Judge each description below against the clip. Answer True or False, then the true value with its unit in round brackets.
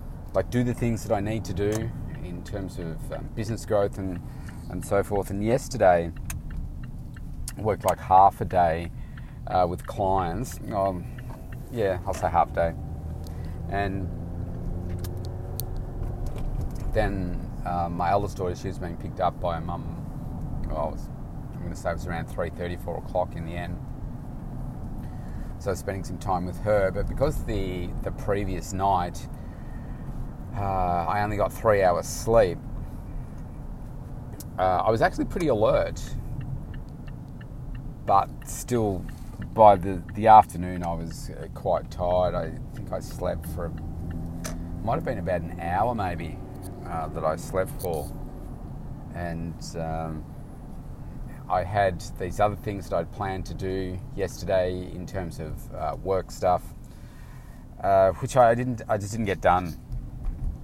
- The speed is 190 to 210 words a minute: False (145 wpm)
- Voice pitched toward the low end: True (95 Hz)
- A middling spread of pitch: True (3.7 semitones)